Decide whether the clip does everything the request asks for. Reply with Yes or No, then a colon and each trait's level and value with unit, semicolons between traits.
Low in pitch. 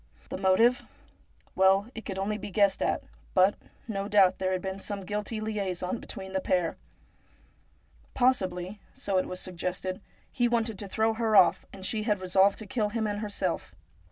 No: high, 200 Hz